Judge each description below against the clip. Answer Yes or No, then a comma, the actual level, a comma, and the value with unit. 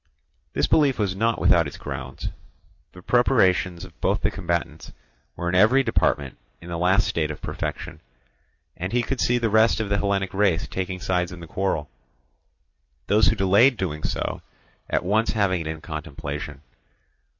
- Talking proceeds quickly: No, average, 170 wpm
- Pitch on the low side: Yes, very low, 95 Hz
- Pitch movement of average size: Yes, average, 4.4 semitones